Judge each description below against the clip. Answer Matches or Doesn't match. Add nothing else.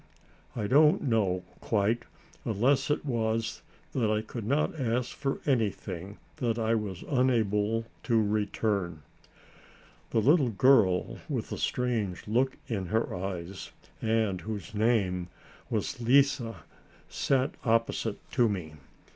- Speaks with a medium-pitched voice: Doesn't match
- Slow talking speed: Matches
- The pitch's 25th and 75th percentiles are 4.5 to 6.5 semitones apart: Doesn't match